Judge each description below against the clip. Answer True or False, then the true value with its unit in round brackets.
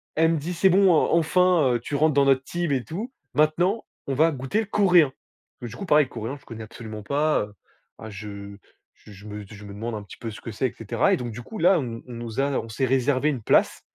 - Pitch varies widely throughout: True (6.2 semitones)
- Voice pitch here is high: False (135 Hz)